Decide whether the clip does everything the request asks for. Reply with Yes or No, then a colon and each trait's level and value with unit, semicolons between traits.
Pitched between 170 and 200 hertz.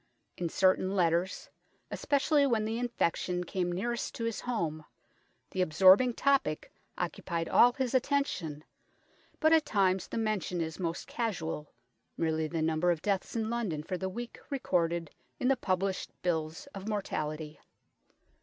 Yes: medium, 185 Hz